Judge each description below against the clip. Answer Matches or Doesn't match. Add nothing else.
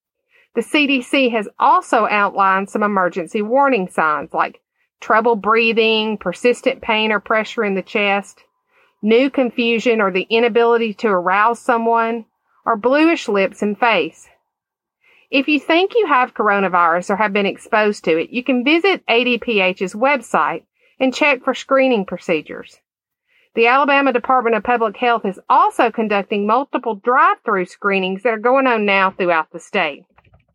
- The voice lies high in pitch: Matches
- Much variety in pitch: Doesn't match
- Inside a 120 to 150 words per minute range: Matches